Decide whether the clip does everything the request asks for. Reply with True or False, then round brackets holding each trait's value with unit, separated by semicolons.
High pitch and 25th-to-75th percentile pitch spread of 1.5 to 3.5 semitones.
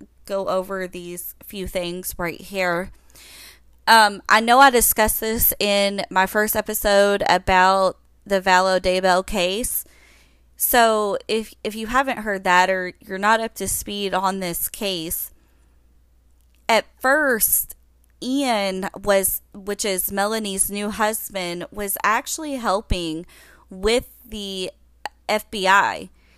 True (195 Hz; 2.8 semitones)